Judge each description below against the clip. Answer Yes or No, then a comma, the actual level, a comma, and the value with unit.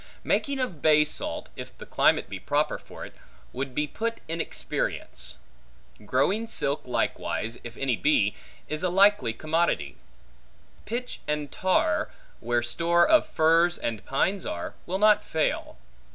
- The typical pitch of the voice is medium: Yes, medium, 155 Hz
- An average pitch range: No, wide, 6.9 semitones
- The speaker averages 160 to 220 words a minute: No, average, 145 wpm